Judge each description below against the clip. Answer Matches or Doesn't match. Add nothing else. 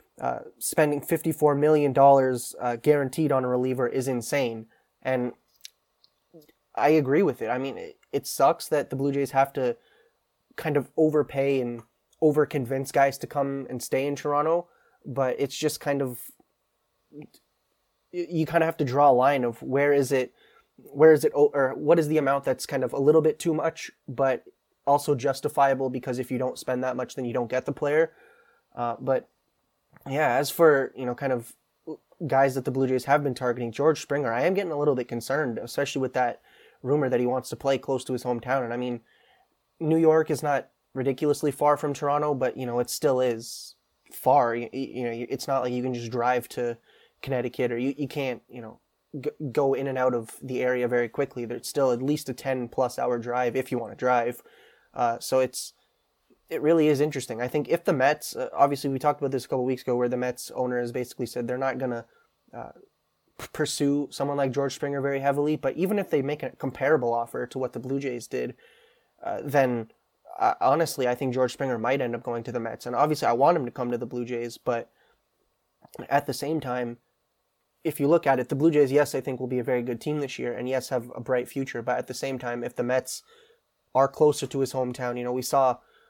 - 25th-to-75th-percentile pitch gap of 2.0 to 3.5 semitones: Matches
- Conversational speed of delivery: Doesn't match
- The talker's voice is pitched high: Doesn't match